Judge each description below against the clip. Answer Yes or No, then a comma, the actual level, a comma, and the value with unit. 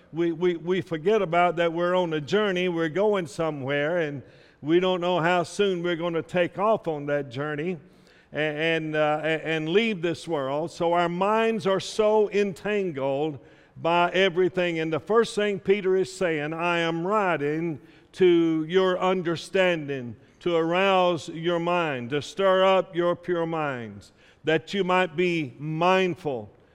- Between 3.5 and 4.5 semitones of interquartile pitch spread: No, average, 2.9 semitones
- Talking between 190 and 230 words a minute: No, average, 155 wpm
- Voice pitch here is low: No, medium, 170 Hz